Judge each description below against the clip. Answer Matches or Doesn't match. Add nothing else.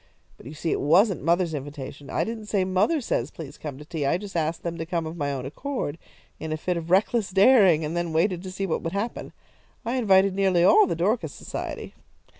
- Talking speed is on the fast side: Matches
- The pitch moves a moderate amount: Matches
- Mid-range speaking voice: Matches